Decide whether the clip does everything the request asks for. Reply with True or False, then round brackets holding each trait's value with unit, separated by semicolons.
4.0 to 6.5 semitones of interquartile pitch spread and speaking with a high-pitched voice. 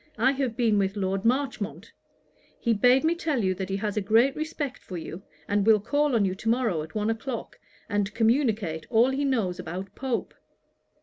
True (5.0 semitones; 225 Hz)